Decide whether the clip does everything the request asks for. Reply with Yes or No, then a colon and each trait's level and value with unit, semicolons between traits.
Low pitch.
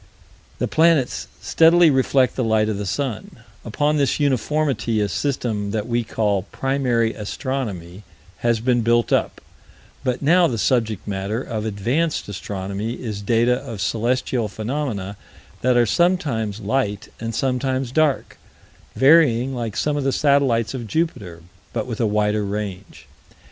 Yes: low, 120 Hz